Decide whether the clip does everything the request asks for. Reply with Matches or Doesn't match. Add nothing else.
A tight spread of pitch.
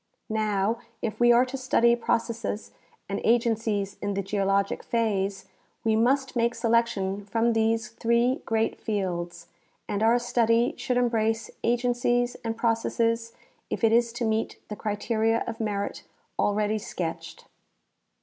Matches